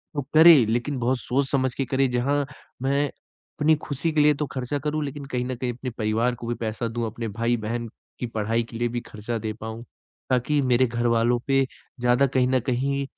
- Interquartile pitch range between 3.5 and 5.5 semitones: No, average, 2.8 semitones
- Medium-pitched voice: No, low, 125 Hz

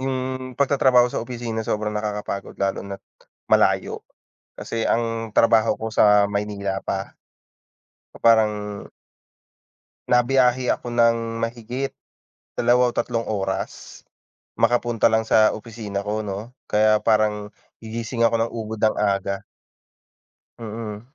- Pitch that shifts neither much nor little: No, narrow, 2.3 semitones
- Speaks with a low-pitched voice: Yes, low, 110 Hz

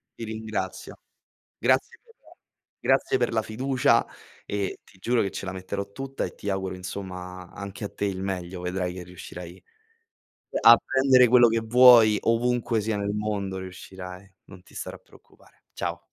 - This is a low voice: Yes, low, 100 Hz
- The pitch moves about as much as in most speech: Yes, average, 3.7 semitones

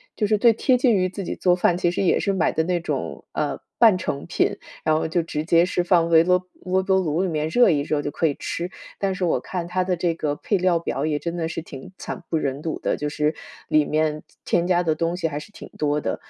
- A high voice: No, medium, 170 Hz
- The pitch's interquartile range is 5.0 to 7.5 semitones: No, average, 3.0 semitones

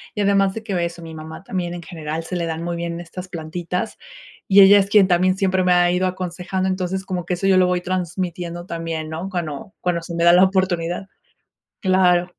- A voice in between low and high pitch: Yes, medium, 180 Hz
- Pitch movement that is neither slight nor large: No, narrow, 1.8 semitones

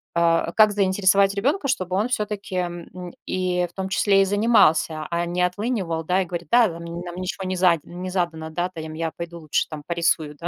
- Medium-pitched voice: Yes, medium, 180 Hz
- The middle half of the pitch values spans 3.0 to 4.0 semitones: No, narrow, 2.5 semitones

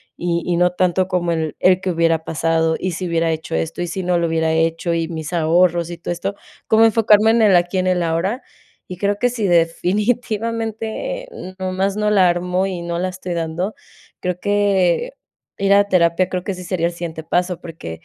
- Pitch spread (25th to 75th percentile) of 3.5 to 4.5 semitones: No, average, 2.9 semitones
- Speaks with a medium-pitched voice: Yes, medium, 180 Hz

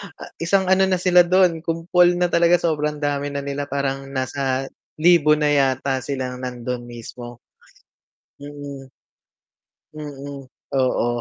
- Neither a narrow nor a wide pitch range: Yes, average, 3.9 semitones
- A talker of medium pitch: Yes, medium, 145 Hz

